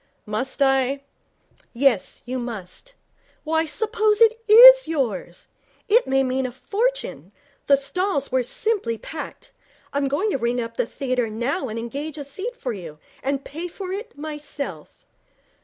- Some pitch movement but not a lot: No, wide, 7.7 semitones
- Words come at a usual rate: Yes, average, 150 wpm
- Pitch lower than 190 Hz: No, very high, 275 Hz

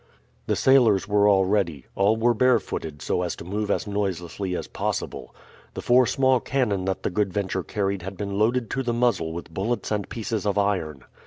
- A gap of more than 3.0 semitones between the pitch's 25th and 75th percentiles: Yes, average, 3.8 semitones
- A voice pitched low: Yes, low, 100 Hz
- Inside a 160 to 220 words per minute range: Yes, average, 195 wpm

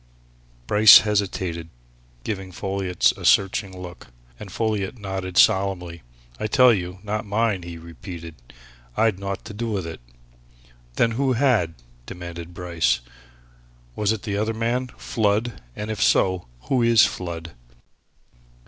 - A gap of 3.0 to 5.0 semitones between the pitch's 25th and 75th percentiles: Yes, average, 3.7 semitones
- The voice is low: Yes, low, 100 Hz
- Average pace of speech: No, slow, 130 wpm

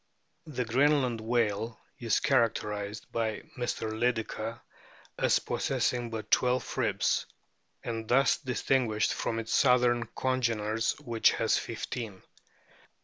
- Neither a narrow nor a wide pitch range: No, narrow, 2.1 semitones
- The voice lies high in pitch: No, low, 115 Hz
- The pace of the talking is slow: Yes, slow, 110 wpm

